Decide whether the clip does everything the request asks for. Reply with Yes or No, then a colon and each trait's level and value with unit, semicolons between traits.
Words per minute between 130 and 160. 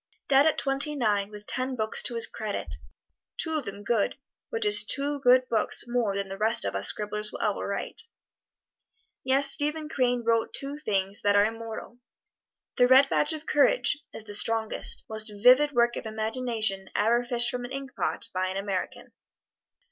No: average, 180 wpm